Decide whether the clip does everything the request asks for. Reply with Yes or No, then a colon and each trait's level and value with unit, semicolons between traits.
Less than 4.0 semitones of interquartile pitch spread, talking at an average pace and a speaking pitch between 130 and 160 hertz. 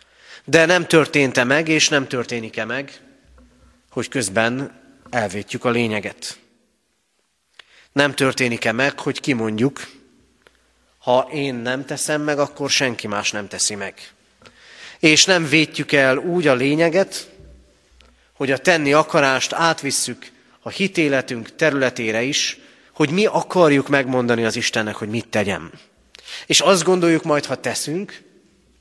No: average, 4.7 semitones; average, 125 wpm; low, 135 Hz